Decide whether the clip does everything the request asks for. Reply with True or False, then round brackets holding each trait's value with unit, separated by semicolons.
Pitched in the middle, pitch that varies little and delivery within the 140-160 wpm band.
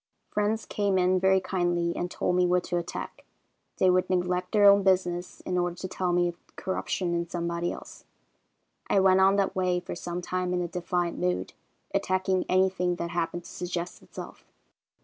False (180 Hz; 1.2 semitones; 185 wpm)